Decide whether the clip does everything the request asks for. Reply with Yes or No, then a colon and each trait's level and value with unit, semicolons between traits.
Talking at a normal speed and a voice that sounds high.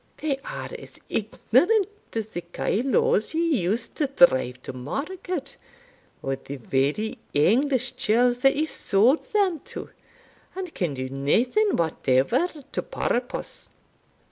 No: slow, 125 wpm; high, 245 Hz